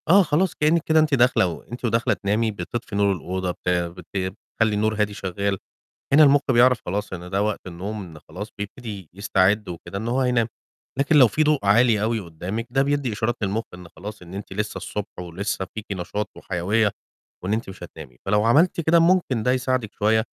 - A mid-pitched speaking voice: No, low, 105 Hz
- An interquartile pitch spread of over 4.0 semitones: Yes, average, 4.7 semitones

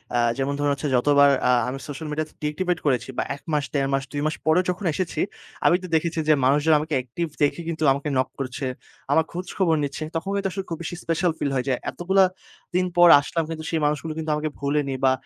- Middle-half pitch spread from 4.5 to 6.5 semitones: No, average, 3.2 semitones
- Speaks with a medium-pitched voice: Yes, medium, 155 Hz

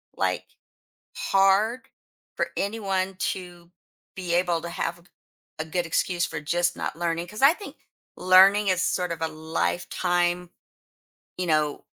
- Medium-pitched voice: Yes, medium, 175 Hz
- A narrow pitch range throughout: Yes, narrow, 2.2 semitones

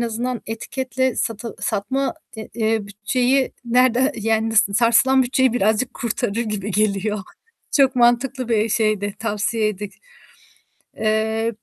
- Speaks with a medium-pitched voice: No, high, 225 Hz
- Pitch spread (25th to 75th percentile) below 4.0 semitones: Yes, average, 2.9 semitones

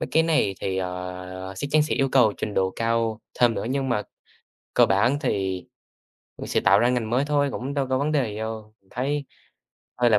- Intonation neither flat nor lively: No, wide, 5.7 semitones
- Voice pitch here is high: No, low, 115 Hz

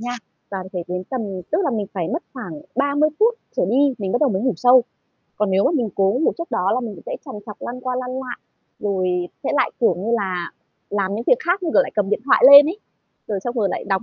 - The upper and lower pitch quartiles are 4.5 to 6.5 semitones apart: Yes, wide, 5.6 semitones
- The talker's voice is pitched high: Yes, high, 240 Hz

